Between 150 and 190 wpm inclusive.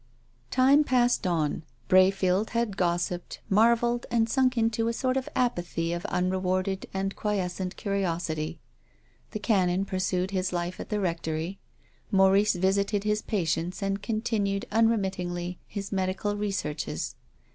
No: slow, 135 wpm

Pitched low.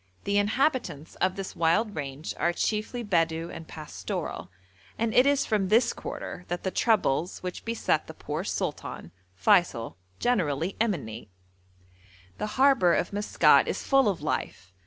No: high, 190 Hz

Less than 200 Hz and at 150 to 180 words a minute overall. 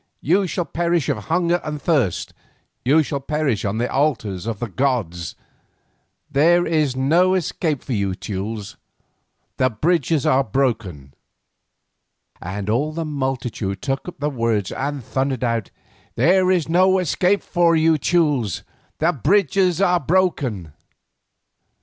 No: medium, 140 Hz; slow, 135 wpm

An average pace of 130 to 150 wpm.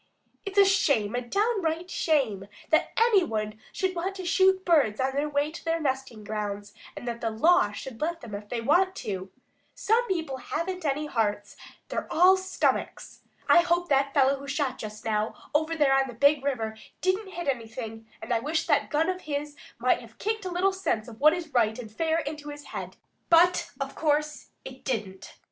No: average, 200 wpm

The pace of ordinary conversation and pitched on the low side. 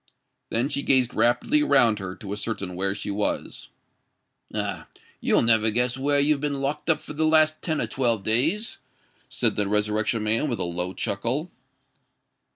Yes: average, 165 wpm; low, 120 Hz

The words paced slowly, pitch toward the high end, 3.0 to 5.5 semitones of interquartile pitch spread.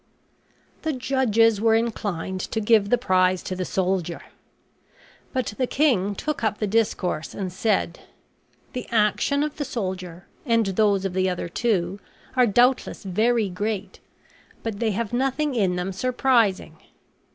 No: average, 145 wpm; high, 210 Hz; average, 4.3 semitones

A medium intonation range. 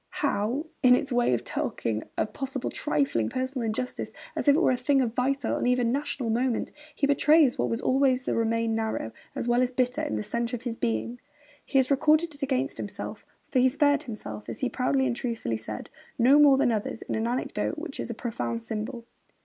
Yes: average, 3.4 semitones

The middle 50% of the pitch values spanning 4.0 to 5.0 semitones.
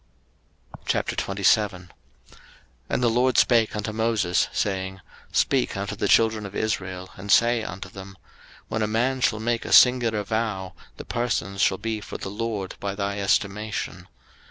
No: average, 2.7 semitones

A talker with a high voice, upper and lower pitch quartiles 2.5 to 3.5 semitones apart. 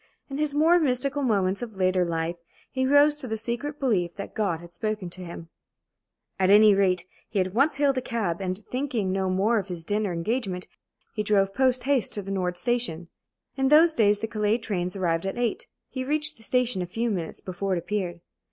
No: high, 210 Hz; wide, 5.5 semitones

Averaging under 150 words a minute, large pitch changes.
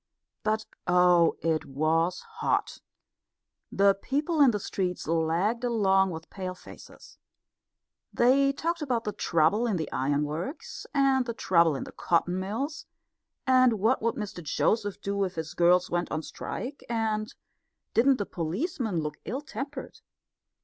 Yes: average, 140 wpm; wide, 6.2 semitones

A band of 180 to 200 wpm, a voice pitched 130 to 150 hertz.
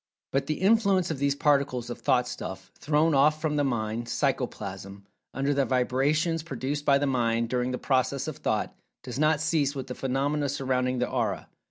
Yes: average, 185 wpm; low, 135 Hz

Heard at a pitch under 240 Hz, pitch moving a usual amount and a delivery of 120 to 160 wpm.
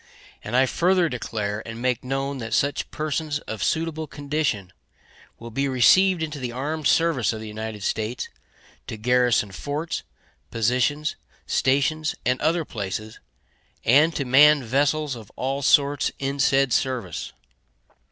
Yes: low, 135 Hz; average, 4.6 semitones; average, 140 wpm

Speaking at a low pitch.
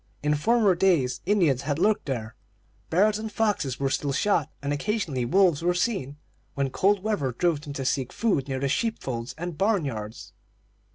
No: medium, 150 Hz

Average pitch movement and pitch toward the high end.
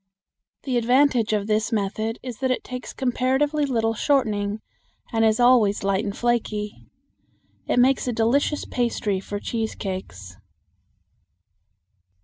Yes: average, 3.3 semitones; high, 225 Hz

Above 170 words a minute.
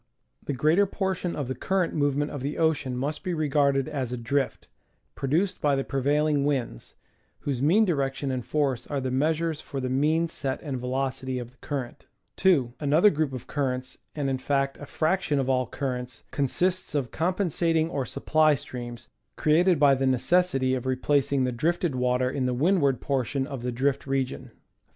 Yes: average, 180 wpm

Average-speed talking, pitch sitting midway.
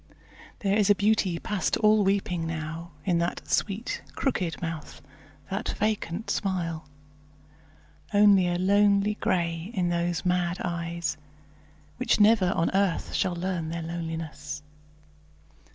No: slow, 120 wpm; medium, 180 Hz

